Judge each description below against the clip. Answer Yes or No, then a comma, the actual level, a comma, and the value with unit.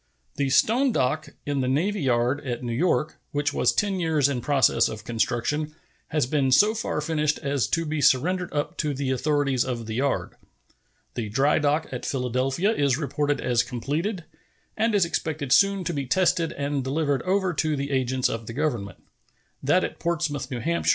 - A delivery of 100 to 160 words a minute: No, average, 185 wpm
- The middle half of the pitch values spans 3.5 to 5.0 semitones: Yes, average, 3.8 semitones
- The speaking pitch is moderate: Yes, medium, 145 Hz